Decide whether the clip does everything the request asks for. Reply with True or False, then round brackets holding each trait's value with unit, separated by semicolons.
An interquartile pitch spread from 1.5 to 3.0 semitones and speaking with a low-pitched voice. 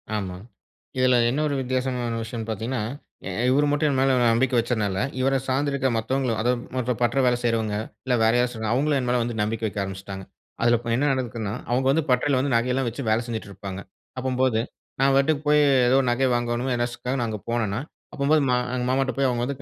True (2.7 semitones; 125 Hz)